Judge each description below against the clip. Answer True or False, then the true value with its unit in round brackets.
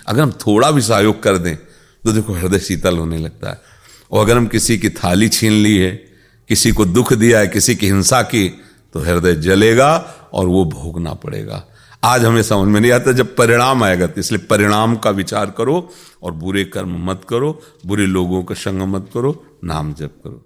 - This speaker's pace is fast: True (200 wpm)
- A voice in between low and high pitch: False (105 Hz)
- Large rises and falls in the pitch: False (3.8 semitones)